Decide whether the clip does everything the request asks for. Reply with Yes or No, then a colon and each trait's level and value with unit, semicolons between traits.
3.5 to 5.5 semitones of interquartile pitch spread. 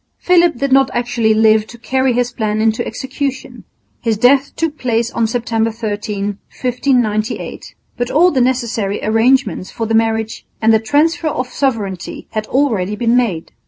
No: average, 3.1 semitones